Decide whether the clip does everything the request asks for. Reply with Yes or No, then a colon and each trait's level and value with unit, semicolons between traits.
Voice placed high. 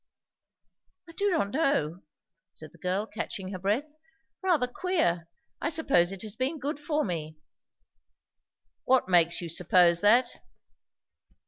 Yes: high, 205 Hz